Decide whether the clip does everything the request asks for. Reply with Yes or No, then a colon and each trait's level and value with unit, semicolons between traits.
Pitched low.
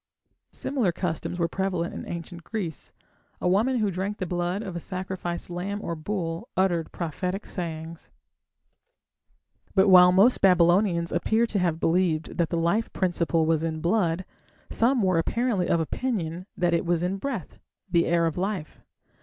No: medium, 180 Hz